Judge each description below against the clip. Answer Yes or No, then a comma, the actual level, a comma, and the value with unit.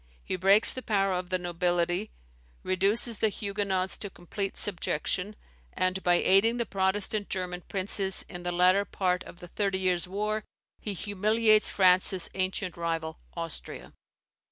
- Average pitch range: No, narrow, 2.3 semitones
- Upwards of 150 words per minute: No, average, 145 wpm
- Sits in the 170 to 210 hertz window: Yes, high, 190 Hz